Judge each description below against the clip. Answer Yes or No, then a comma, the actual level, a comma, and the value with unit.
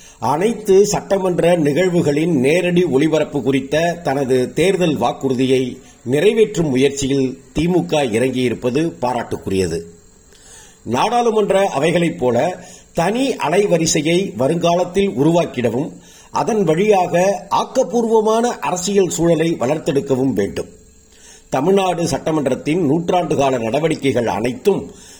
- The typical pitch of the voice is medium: Yes, medium, 160 Hz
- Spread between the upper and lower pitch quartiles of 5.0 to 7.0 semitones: Yes, wide, 5.5 semitones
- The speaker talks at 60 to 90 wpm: Yes, average, 80 wpm